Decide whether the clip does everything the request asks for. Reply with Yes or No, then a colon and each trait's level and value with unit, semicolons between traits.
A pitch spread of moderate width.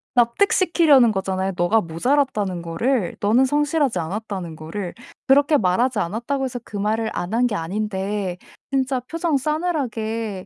No: wide, 6.0 semitones